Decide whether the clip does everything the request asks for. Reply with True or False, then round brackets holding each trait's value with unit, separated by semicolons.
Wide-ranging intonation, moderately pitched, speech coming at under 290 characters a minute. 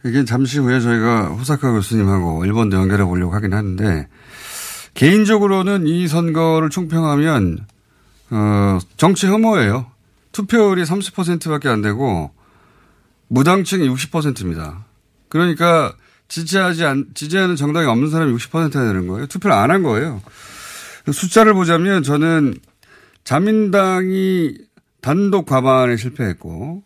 True (8.7 semitones; 145 Hz; 275 characters per minute)